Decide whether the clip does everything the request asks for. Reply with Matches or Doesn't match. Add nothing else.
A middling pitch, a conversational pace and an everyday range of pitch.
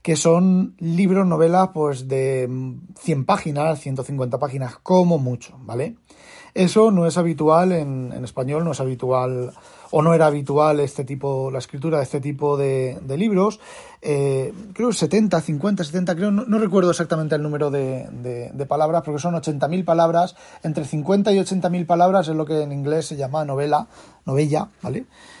Matches